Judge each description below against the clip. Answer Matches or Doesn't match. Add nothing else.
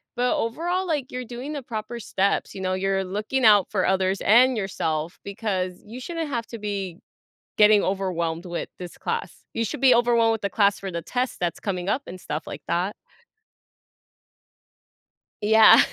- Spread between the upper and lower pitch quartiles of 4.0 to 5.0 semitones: Matches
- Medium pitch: Doesn't match